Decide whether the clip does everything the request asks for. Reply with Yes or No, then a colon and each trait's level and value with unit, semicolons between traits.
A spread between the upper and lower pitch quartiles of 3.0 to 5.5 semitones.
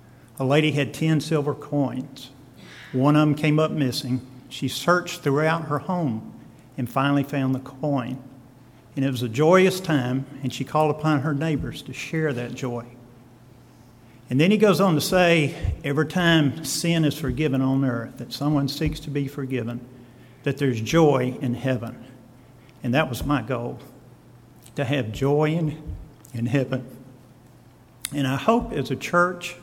Yes: average, 3.3 semitones